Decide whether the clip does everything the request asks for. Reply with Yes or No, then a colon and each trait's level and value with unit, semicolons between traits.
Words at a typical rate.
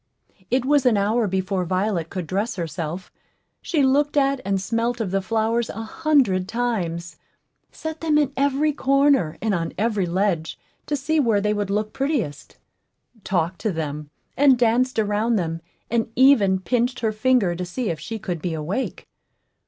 Yes: average, 170 wpm